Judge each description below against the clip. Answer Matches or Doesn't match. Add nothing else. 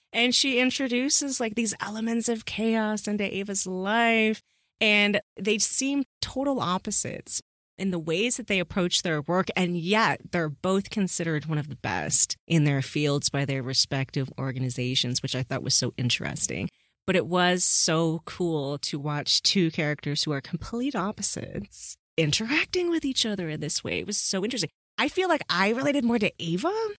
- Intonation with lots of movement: Matches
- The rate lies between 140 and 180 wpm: Matches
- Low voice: Doesn't match